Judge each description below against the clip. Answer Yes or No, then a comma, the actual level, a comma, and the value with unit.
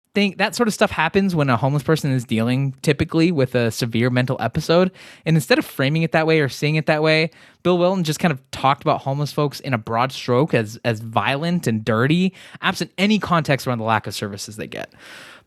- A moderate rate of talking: No, fast, 220 wpm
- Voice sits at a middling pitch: Yes, medium, 145 Hz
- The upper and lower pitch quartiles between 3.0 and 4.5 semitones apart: No, average, 5.0 semitones